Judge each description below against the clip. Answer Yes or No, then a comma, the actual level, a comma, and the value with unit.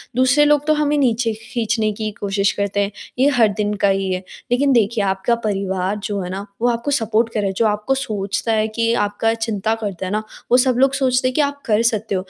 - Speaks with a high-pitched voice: Yes, high, 220 Hz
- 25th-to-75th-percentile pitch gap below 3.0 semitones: No, average, 3.6 semitones